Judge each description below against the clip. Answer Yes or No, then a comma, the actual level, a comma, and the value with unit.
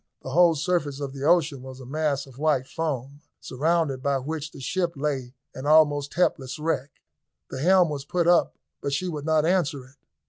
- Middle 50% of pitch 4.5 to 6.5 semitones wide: No, average, 3.1 semitones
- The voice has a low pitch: No, medium, 145 Hz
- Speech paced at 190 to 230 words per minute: Yes, average, 195 wpm